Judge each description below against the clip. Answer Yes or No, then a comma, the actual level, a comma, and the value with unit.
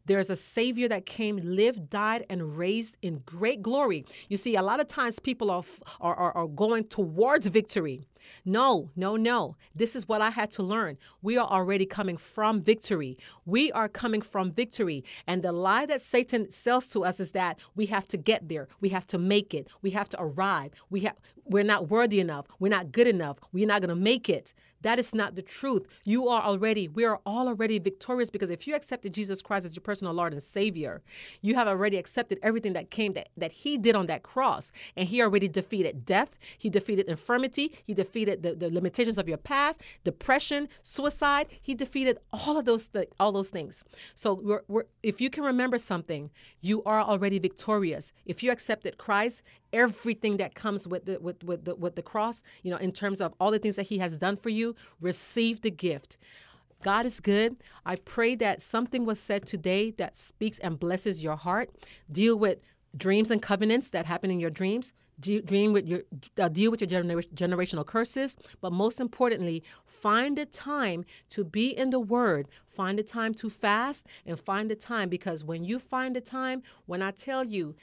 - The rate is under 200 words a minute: No, fast, 205 wpm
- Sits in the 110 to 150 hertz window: No, high, 205 Hz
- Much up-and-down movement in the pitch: No, average, 4.0 semitones